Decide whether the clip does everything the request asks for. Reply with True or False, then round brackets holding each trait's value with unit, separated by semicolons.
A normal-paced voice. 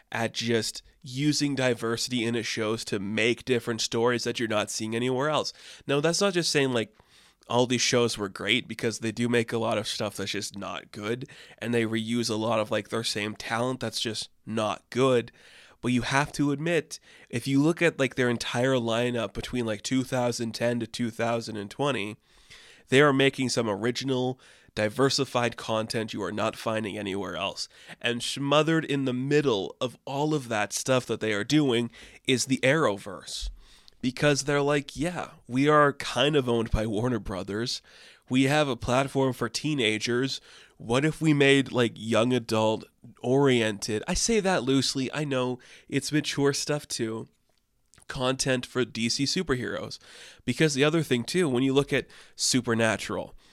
True (170 wpm)